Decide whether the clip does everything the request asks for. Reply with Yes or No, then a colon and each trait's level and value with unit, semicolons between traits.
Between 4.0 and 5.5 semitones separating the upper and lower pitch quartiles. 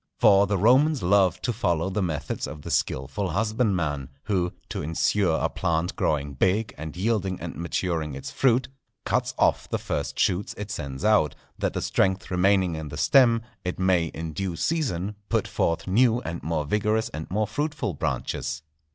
Yes: average, 4.8 semitones